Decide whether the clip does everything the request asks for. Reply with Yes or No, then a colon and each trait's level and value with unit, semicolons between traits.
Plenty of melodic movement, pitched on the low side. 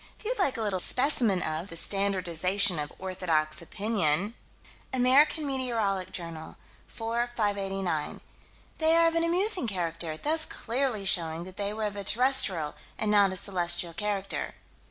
No: wide, 5.9 semitones; high, 200 Hz